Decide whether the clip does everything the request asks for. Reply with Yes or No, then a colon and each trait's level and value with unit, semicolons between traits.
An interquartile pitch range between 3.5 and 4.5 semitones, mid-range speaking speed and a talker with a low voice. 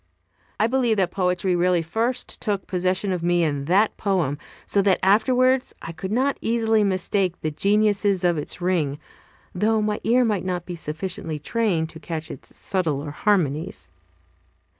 No: average, 4.0 semitones; average, 160 wpm; medium, 185 Hz